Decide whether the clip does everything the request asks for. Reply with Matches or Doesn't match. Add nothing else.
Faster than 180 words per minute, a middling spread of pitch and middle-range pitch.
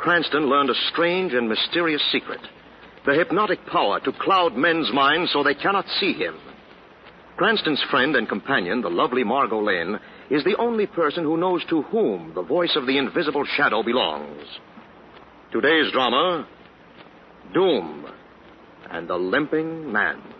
Doesn't match